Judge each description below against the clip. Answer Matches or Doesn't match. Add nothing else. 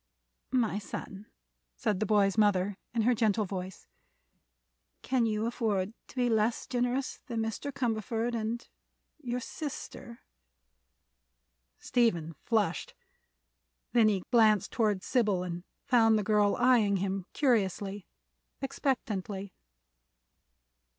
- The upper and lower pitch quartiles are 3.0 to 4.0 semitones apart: Matches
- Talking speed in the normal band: Doesn't match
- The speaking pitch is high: Matches